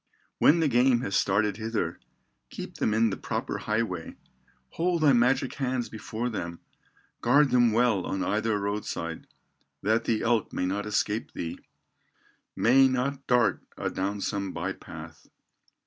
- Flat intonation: No, average, 3.6 semitones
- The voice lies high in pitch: No, low, 110 Hz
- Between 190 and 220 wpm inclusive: No, average, 145 wpm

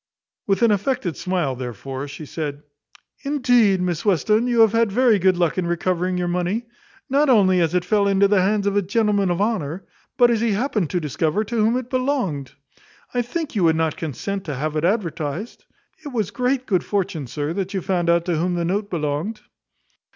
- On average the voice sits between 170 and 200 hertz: Yes, high, 190 Hz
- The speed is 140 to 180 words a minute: No, average, 200 wpm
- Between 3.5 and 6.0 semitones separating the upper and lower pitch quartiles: Yes, average, 4.8 semitones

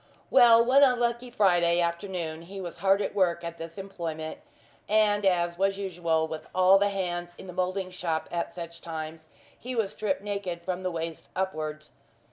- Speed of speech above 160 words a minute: Yes, average, 175 wpm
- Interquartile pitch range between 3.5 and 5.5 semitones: No, average, 2.8 semitones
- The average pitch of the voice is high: No, medium, 180 Hz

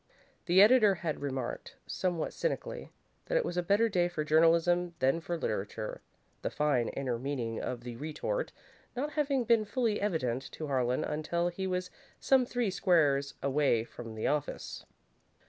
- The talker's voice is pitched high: No, medium, 165 Hz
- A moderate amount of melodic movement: No, wide, 6.5 semitones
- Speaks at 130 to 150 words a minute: No, average, 160 wpm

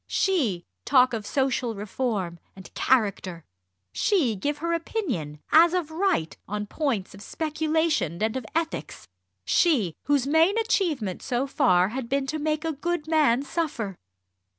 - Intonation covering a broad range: Yes, wide, 7.4 semitones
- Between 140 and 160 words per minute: Yes, average, 145 wpm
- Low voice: No, very high, 270 Hz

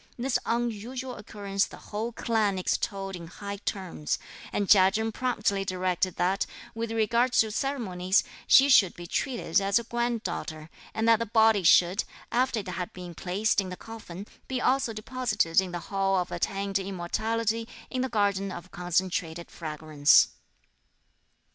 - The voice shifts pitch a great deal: No, average, 3.9 semitones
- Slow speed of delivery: No, average, 155 wpm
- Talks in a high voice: Yes, high, 200 Hz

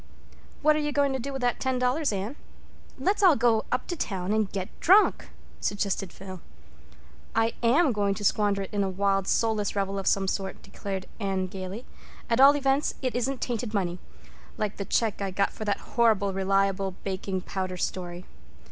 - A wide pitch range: No, average, 4.4 semitones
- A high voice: Yes, high, 200 Hz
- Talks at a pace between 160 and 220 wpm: Yes, average, 180 wpm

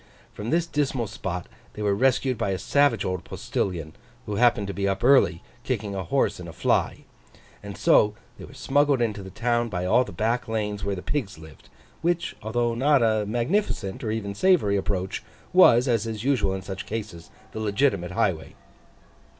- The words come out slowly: No, average, 180 wpm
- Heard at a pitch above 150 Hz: No, low, 110 Hz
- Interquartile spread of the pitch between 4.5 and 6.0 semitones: No, average, 4.0 semitones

